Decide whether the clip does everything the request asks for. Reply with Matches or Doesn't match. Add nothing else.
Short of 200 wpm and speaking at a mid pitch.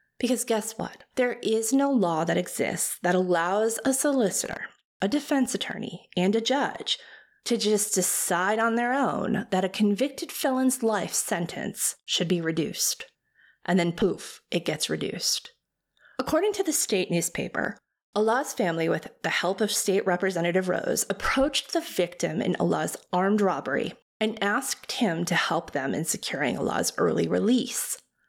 Doesn't match